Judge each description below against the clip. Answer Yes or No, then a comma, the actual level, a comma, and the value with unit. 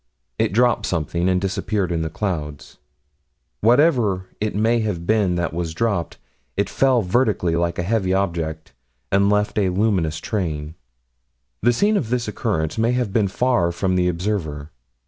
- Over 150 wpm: Yes, average, 160 wpm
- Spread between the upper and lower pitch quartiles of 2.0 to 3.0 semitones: No, average, 4.4 semitones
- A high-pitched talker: No, very low, 95 Hz